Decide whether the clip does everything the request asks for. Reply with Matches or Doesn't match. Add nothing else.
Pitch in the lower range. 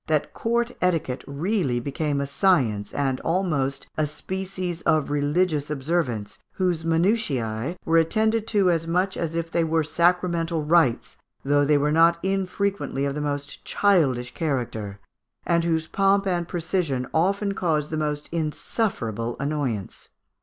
Doesn't match